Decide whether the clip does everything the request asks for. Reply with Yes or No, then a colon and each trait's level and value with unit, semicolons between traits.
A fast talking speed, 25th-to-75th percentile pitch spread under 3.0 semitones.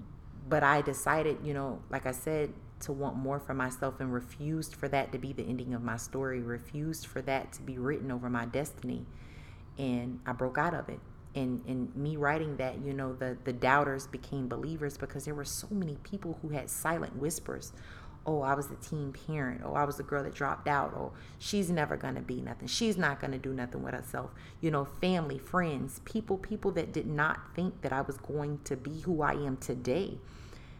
Yes: fast, 215 wpm; narrow, 2.6 semitones